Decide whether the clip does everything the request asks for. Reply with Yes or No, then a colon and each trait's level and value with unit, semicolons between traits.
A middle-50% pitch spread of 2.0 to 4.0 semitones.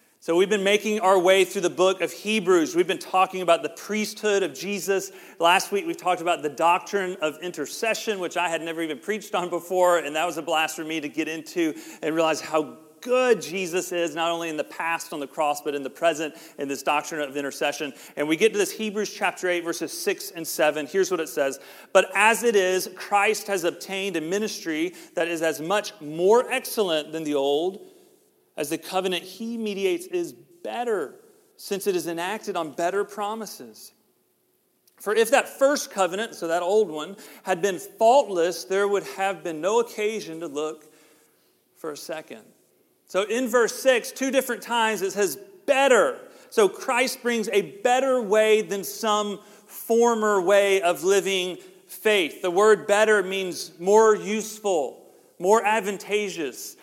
No: average, 4.9 semitones